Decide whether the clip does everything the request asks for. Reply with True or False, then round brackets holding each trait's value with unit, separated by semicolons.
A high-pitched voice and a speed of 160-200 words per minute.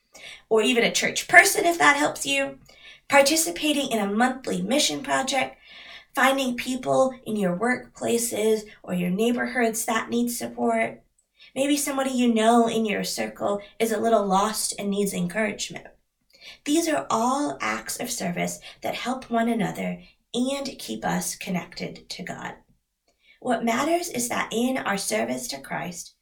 False (230 Hz; 150 wpm)